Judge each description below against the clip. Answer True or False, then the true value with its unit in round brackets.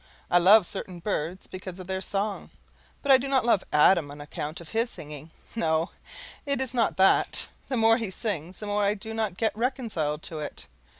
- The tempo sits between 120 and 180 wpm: False (200 wpm)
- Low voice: False (195 Hz)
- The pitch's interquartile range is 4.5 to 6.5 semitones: True (5.0 semitones)